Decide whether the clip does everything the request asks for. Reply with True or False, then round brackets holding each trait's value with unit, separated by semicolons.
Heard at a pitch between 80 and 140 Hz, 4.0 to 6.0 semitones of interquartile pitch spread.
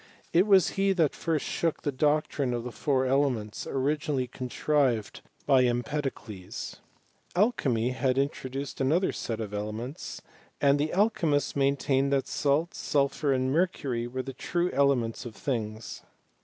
False (135 Hz; 3.4 semitones)